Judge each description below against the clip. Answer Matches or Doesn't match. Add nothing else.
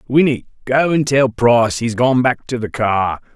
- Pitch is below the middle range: Matches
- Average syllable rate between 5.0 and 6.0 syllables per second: Doesn't match